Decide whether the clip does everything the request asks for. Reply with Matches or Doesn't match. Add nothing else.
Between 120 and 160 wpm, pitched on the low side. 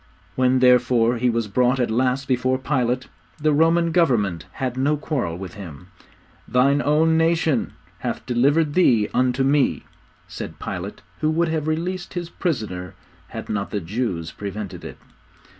Matches